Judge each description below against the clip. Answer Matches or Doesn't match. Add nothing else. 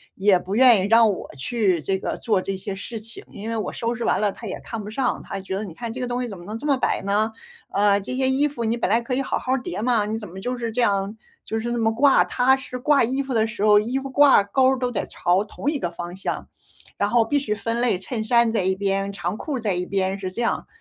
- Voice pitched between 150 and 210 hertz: Doesn't match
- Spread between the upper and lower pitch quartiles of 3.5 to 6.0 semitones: Matches